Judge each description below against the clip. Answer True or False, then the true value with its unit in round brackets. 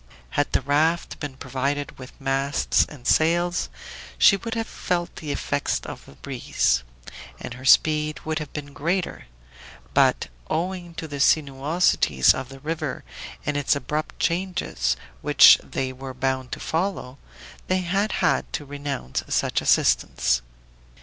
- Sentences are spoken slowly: False (145 wpm)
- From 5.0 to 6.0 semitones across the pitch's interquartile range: False (4.0 semitones)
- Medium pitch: True (145 Hz)